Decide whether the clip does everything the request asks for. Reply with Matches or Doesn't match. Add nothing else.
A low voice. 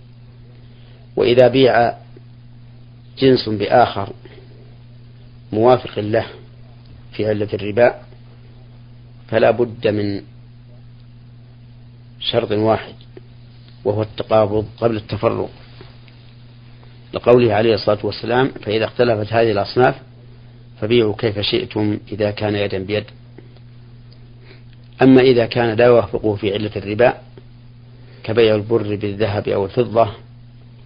Matches